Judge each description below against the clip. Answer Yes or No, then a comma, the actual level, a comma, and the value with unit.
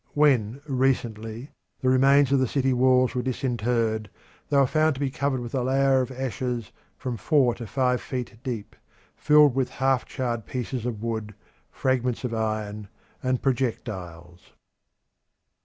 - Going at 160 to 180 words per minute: No, average, 150 wpm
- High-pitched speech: No, low, 125 Hz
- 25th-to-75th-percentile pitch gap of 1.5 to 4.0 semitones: Yes, average, 2.7 semitones